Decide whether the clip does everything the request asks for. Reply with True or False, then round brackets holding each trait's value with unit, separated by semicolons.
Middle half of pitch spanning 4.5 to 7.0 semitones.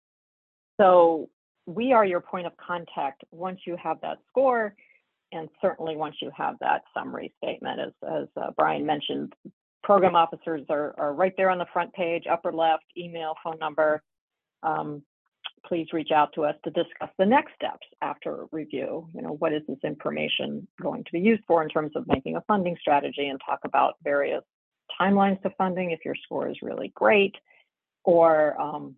False (3.2 semitones)